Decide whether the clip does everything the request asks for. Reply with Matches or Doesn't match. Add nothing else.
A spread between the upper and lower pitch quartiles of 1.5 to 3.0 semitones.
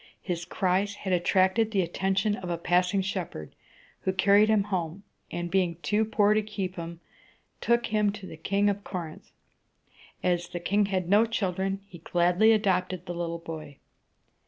Matches